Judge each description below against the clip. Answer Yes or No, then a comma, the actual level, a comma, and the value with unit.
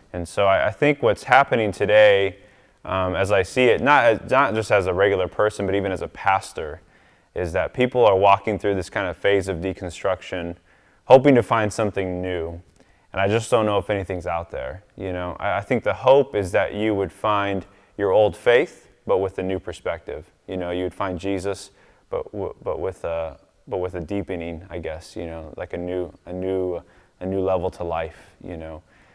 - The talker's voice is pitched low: Yes, very low, 95 Hz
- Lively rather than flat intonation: No, average, 2.7 semitones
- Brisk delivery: Yes, fast, 210 wpm